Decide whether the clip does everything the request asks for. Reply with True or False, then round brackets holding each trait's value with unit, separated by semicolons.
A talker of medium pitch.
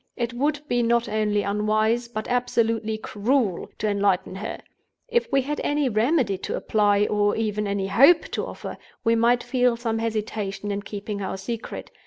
False (220 Hz)